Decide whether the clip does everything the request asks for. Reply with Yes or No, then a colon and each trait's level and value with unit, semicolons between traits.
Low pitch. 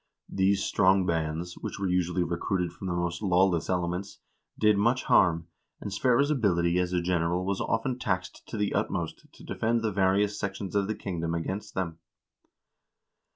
Yes: very low, 95 Hz